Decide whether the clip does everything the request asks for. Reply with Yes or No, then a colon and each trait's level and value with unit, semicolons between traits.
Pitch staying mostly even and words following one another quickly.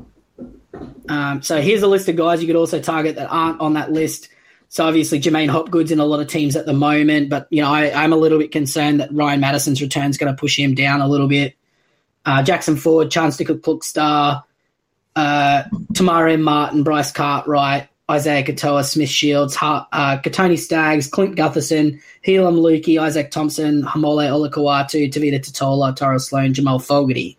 No: narrow, 2.0 semitones; average, 185 wpm